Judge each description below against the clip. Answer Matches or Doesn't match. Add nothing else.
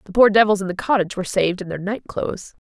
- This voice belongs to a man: Doesn't match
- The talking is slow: Doesn't match